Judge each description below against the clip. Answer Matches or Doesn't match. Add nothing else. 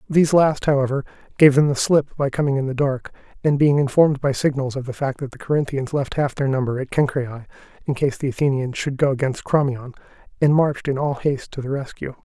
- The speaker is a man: Matches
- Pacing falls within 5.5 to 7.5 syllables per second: Matches